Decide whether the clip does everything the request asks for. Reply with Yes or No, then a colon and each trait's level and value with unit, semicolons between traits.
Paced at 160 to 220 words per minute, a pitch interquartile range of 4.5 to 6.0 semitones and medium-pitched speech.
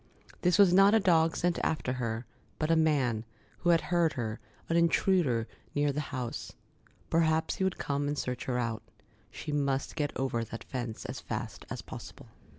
Yes: average, 180 wpm; average, 5.1 semitones; medium, 145 Hz